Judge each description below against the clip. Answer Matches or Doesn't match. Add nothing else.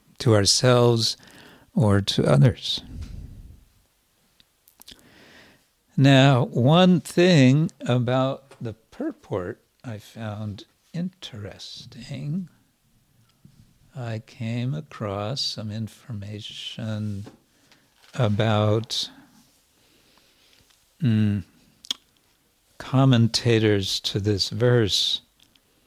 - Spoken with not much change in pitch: Doesn't match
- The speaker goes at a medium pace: Doesn't match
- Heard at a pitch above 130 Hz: Doesn't match